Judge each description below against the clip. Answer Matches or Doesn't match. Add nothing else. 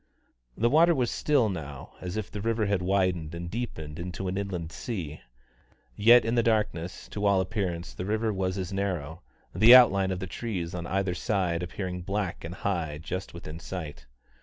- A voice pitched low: Matches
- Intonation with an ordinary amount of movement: Matches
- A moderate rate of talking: Matches